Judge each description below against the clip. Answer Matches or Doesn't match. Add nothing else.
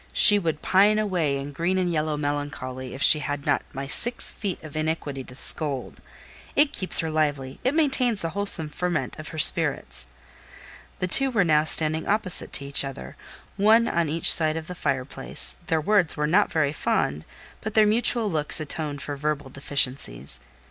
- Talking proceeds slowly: Doesn't match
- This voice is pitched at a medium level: Matches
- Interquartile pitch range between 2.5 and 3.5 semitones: Doesn't match